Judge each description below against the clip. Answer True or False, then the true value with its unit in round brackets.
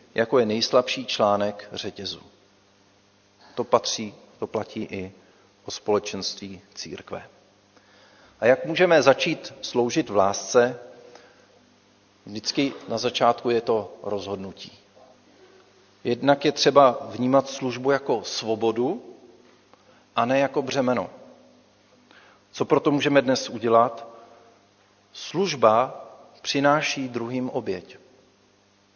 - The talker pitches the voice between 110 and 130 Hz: True (115 Hz)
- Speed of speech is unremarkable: False (95 wpm)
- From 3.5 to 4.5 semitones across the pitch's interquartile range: False (5.1 semitones)